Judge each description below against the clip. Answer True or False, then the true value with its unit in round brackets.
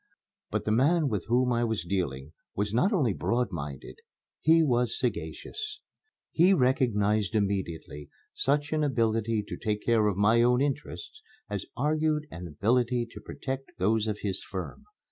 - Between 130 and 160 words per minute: True (155 wpm)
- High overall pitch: False (115 Hz)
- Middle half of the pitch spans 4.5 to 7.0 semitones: True (5.1 semitones)